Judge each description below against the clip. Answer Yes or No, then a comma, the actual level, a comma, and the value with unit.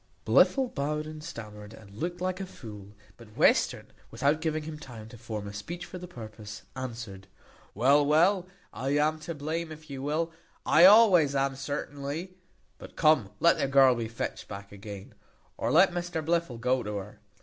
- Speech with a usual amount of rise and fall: No, wide, 6.4 semitones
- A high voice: No, medium, 140 Hz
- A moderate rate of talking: Yes, average, 180 wpm